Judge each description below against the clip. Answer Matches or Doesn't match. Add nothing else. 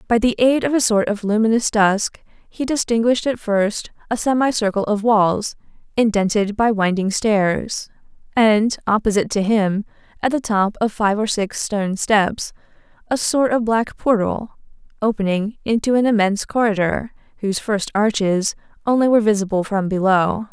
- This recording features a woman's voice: Matches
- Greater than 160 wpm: Doesn't match